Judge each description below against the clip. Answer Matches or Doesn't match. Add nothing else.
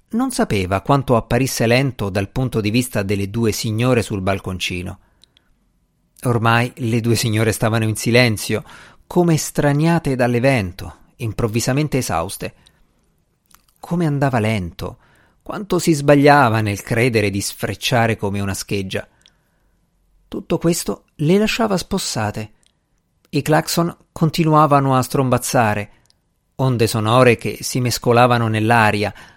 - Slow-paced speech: Matches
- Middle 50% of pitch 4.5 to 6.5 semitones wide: Matches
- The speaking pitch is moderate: Doesn't match